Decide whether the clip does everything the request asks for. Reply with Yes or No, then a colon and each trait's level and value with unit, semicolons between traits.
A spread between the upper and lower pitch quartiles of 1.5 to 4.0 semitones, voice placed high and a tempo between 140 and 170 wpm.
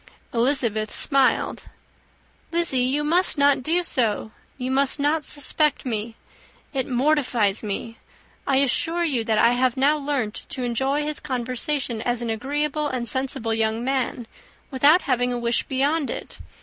Yes: average, 3.6 semitones; very high, 260 Hz; average, 150 wpm